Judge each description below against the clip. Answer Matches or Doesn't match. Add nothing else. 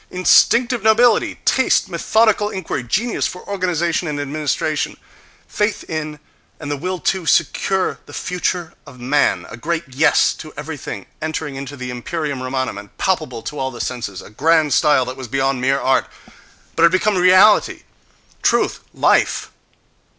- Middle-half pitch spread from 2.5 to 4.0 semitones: Doesn't match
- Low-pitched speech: Doesn't match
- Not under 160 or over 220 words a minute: Doesn't match